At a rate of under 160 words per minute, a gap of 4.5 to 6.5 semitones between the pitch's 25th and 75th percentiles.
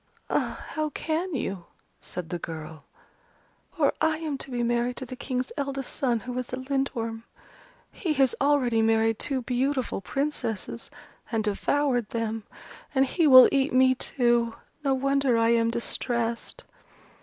No: average, 150 wpm; average, 3.3 semitones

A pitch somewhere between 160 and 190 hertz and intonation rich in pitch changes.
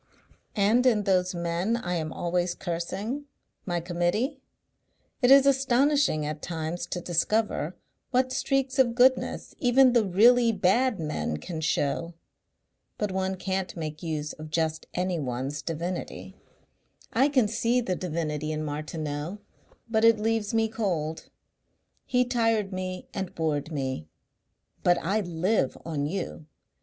Yes: medium, 185 Hz; wide, 6.1 semitones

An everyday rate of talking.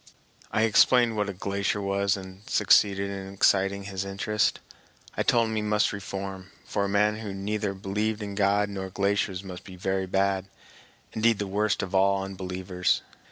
Yes: average, 170 wpm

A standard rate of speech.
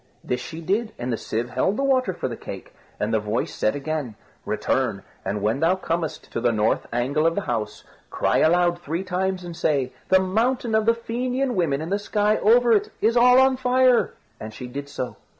No: fast, 210 wpm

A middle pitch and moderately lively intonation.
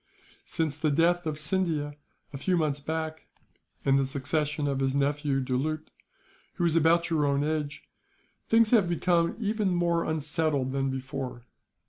Yes: medium, 155 Hz; average, 3.3 semitones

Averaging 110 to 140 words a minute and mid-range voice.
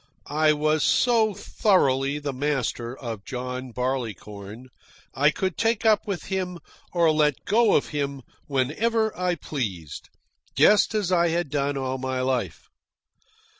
Yes: slow, 135 wpm; medium, 145 Hz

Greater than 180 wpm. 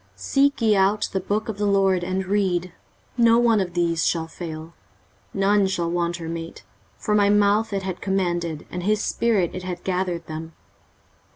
Yes: average, 190 wpm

